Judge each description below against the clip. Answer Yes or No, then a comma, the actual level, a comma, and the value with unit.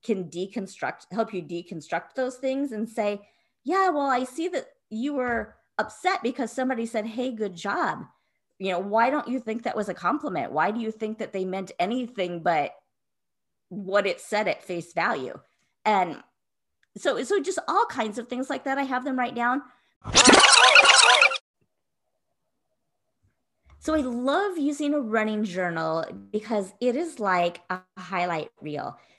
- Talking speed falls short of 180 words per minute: Yes, average, 160 wpm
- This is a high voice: Yes, high, 225 Hz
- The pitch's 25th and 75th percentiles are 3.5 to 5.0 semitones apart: No, wide, 5.5 semitones